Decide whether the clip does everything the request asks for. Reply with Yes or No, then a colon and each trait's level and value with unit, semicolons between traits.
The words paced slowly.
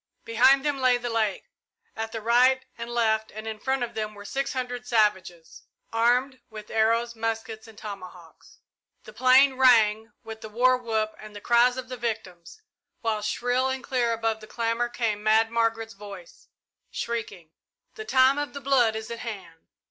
No: average, 175 wpm